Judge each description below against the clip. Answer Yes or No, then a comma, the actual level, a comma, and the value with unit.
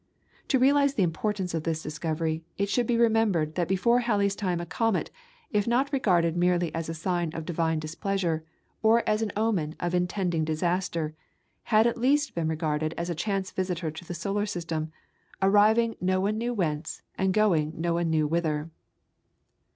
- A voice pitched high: No, medium, 180 Hz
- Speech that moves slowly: No, average, 175 wpm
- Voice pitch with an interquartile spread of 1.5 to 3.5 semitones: No, average, 4.7 semitones